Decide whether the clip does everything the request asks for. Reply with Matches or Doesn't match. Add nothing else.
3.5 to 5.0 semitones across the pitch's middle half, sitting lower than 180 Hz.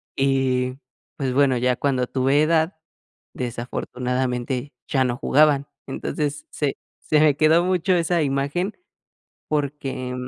Doesn't match